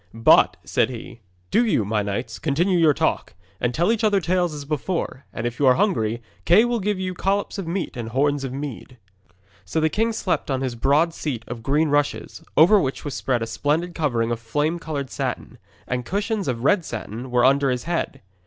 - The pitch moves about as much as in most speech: No, wide, 6.3 semitones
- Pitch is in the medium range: Yes, medium, 145 Hz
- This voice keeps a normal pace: No, fast, 210 wpm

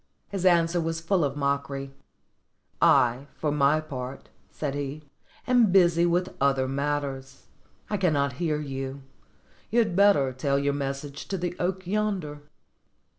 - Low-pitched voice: No, medium, 145 Hz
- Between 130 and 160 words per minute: Yes, average, 140 wpm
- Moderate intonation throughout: Yes, average, 4.3 semitones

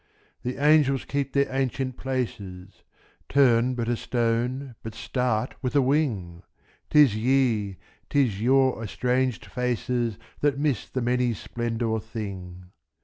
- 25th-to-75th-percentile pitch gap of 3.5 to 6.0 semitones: No, average, 3.1 semitones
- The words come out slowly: Yes, slow, 120 wpm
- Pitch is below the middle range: Yes, low, 125 Hz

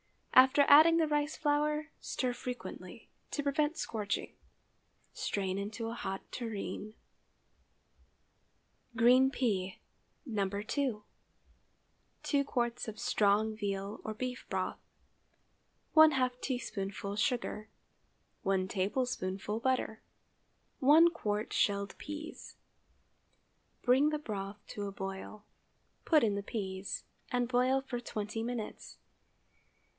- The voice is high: Yes, high, 230 Hz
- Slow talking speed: Yes, slow, 105 wpm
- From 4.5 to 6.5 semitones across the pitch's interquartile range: Yes, average, 4.8 semitones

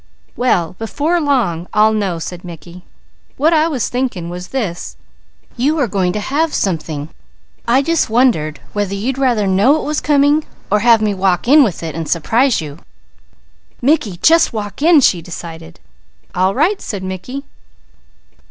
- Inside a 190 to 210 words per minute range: No, average, 160 wpm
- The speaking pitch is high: Yes, high, 215 Hz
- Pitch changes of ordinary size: No, wide, 7.6 semitones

